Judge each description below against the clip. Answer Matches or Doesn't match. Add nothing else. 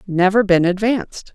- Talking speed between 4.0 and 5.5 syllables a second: Matches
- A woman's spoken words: Matches